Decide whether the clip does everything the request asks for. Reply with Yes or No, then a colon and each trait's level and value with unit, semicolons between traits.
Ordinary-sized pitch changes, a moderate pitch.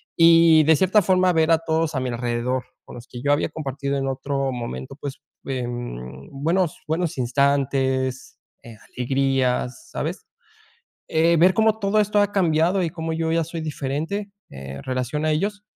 Yes: average, 4.5 semitones; medium, 145 Hz